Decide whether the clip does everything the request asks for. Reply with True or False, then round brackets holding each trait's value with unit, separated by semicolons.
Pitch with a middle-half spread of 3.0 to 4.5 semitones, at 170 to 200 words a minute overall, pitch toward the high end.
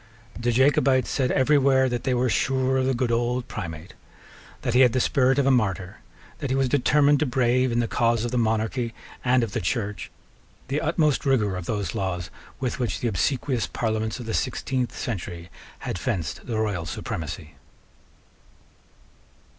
False (3.5 semitones; 180 wpm; 120 Hz)